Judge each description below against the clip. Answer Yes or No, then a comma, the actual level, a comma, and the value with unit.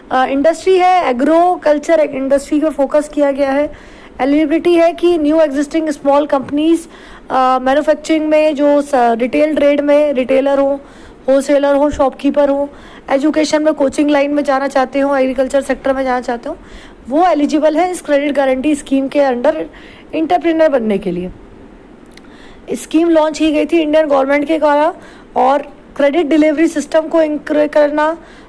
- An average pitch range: No, narrow, 2.1 semitones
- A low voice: No, very high, 290 Hz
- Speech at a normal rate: Yes, average, 155 wpm